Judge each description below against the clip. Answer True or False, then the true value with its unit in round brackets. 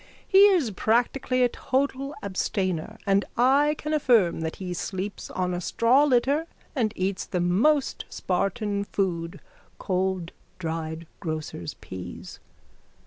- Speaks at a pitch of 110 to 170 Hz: False (200 Hz)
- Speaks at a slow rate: True (125 wpm)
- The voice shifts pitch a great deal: True (6.5 semitones)